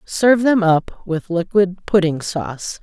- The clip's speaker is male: No, female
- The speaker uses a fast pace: No, average, 150 wpm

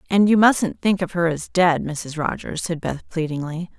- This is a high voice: No, medium, 170 Hz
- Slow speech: No, fast, 205 wpm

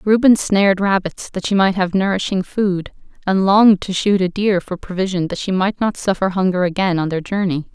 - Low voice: No, high, 190 Hz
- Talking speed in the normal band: No, fast, 210 wpm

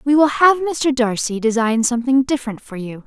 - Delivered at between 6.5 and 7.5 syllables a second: No, 5.4 syllables/s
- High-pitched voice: Yes, very high, 250 Hz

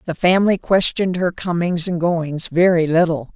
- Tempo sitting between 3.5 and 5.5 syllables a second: Yes, 5.0 syllables/s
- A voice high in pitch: No, medium, 170 Hz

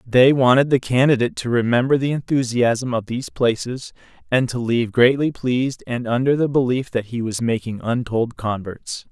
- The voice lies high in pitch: No, low, 125 Hz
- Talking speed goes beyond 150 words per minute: Yes, average, 170 wpm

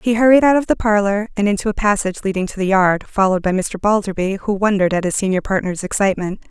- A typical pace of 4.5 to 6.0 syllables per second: No, 6.9 syllables/s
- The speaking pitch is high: Yes, high, 200 Hz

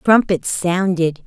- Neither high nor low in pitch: Yes, medium, 180 Hz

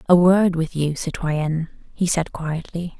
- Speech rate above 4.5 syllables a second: No, 4.3 syllables/s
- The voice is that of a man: No, female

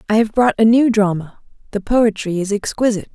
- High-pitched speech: Yes, high, 215 Hz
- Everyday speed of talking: Yes, average, 190 wpm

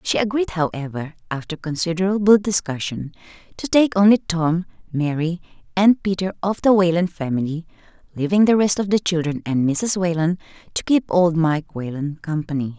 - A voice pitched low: No, medium, 175 Hz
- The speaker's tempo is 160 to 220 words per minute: No, average, 150 wpm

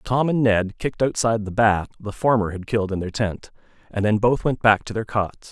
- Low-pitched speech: Yes, low, 110 Hz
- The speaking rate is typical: No, fast, 240 wpm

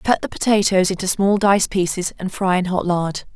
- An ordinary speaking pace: No, fast, 215 wpm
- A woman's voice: Yes, female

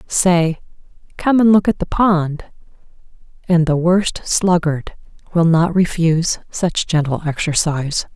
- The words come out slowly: Yes, slow, 125 wpm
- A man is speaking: No, female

